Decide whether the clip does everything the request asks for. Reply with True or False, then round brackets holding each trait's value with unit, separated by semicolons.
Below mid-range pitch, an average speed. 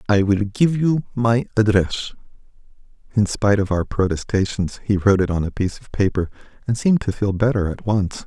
True (105 Hz; 190 wpm)